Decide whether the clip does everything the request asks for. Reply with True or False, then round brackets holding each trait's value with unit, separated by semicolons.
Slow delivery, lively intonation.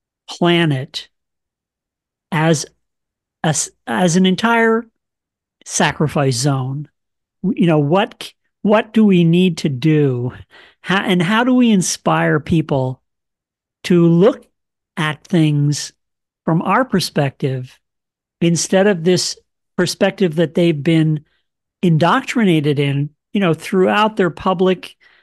False (105 wpm; 4.3 semitones)